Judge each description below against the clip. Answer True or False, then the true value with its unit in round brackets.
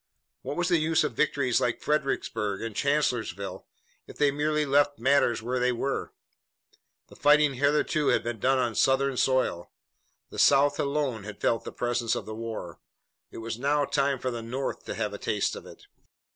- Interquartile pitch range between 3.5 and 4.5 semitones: True (3.9 semitones)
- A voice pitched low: True (130 Hz)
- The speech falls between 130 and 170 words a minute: False (180 wpm)